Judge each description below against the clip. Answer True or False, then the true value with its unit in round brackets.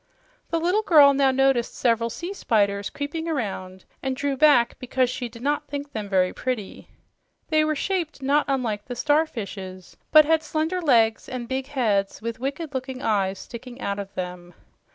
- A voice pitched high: True (255 Hz)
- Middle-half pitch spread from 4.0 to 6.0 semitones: True (5.2 semitones)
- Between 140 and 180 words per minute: True (175 wpm)